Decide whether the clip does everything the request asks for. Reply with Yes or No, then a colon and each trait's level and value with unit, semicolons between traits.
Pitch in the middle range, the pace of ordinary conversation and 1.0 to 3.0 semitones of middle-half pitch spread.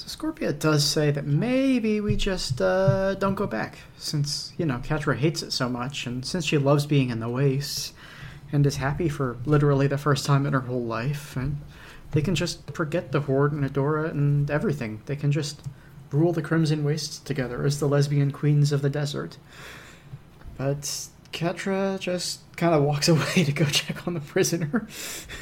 Yes: medium, 145 Hz; average, 185 wpm; average, 2.7 semitones